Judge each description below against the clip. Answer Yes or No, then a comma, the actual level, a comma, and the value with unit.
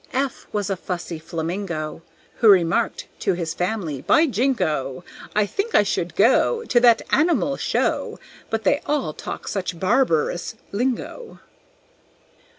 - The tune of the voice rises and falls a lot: Yes, wide, 7.2 semitones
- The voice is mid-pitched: No, high, 200 Hz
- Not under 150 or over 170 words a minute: No, slow, 135 wpm